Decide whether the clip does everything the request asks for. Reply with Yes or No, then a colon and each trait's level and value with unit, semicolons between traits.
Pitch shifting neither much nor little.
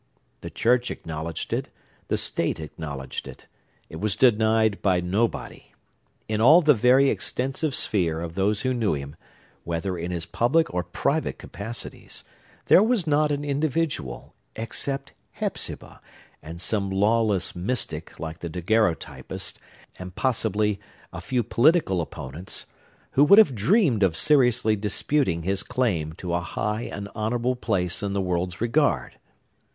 No: wide, 6.3 semitones